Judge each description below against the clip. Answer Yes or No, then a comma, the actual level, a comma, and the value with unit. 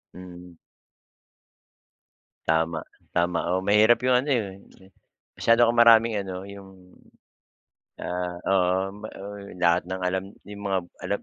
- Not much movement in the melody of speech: Yes, narrow, 2.2 semitones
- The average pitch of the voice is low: Yes, very low, 95 Hz